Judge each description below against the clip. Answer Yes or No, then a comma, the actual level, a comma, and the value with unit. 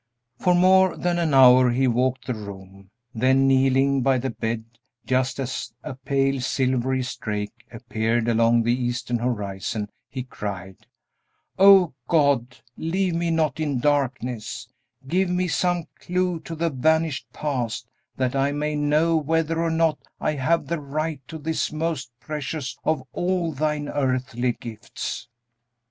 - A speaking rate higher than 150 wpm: No, average, 145 wpm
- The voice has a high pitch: No, low, 135 Hz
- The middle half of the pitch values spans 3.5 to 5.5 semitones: Yes, average, 4.6 semitones